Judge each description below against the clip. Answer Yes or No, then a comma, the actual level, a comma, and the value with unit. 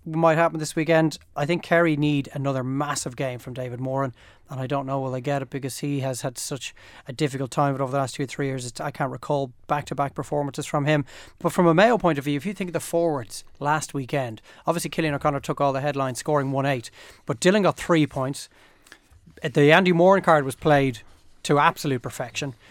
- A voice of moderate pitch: Yes, medium, 145 Hz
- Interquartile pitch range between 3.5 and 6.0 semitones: No, average, 2.9 semitones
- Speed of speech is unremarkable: No, fast, 225 wpm